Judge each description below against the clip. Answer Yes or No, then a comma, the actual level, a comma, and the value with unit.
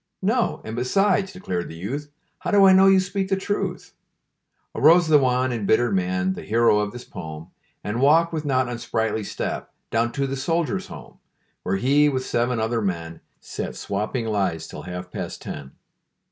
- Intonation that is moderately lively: No, wide, 7.9 semitones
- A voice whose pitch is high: No, low, 125 Hz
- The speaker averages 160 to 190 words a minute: Yes, average, 175 wpm